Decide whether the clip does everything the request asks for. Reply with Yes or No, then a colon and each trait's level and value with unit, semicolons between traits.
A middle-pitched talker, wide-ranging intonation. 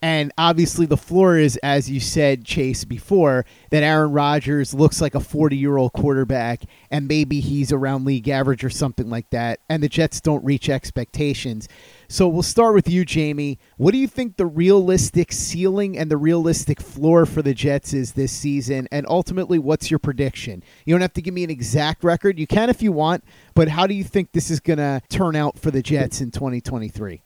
No: medium, 150 Hz; average, 3.9 semitones